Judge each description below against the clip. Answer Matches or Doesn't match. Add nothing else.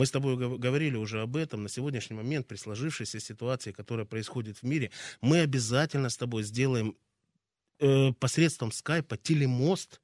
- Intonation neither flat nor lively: Matches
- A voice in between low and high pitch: Doesn't match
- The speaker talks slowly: Doesn't match